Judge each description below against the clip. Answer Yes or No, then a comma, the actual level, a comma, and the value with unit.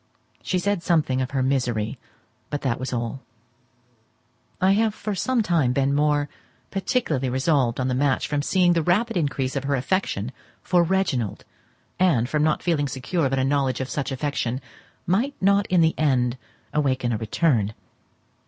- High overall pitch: No, medium, 145 Hz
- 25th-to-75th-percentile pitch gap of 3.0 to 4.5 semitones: No, average, 5.3 semitones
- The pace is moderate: Yes, average, 165 wpm